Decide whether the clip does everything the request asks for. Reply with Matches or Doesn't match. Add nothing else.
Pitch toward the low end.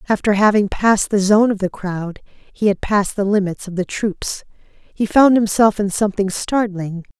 Doesn't match